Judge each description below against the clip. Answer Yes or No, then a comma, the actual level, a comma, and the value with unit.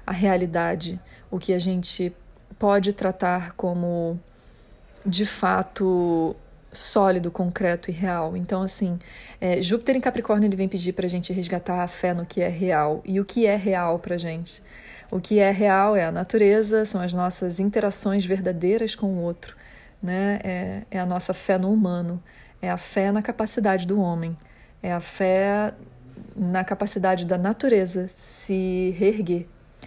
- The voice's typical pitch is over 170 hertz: Yes, medium, 185 Hz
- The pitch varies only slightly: Yes, narrow, 2.2 semitones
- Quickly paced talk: No, average, 165 wpm